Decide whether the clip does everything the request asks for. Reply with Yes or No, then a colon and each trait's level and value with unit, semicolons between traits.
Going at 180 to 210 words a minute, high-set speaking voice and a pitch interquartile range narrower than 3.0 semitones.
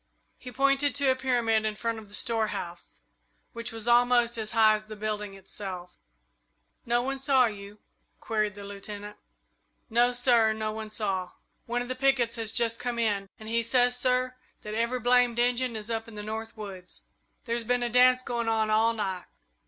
Yes: average, 185 wpm; high, 230 Hz; narrow, 2.5 semitones